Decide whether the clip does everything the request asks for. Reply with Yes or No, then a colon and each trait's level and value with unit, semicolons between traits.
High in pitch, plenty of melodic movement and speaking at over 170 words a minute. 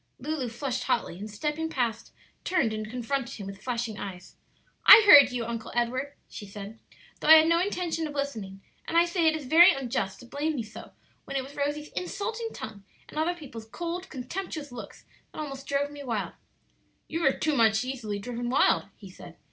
Yes: very high, 265 Hz; wide, 5.8 semitones; average, 195 wpm